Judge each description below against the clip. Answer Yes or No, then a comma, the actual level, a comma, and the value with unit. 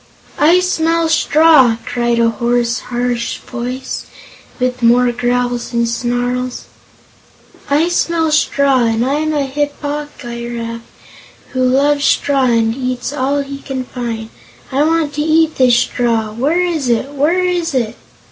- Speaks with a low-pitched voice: No, very high, 255 Hz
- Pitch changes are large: No, average, 3.6 semitones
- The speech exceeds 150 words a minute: No, average, 145 wpm